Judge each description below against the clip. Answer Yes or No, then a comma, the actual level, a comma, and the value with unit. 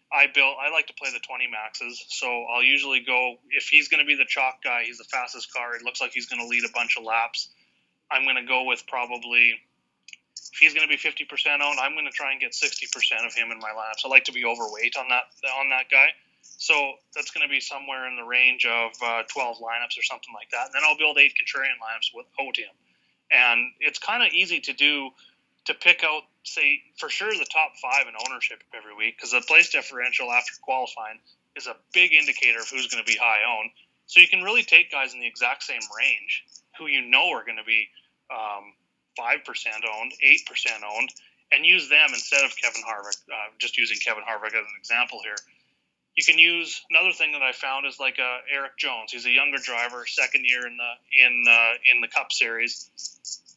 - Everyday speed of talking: No, fast, 225 wpm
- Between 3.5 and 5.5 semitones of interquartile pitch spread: No, narrow, 2.6 semitones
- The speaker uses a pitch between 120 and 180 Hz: Yes, low, 125 Hz